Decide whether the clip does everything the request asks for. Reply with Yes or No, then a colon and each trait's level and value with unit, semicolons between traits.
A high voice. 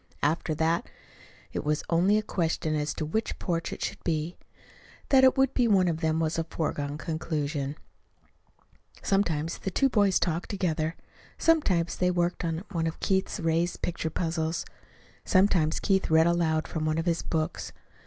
No: medium, 165 Hz